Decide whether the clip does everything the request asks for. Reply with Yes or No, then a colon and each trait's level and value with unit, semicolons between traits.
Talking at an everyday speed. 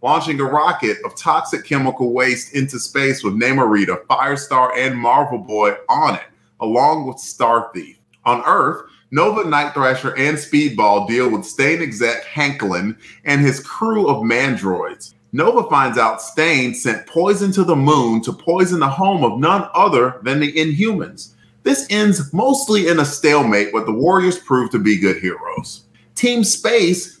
Yes: average, 160 wpm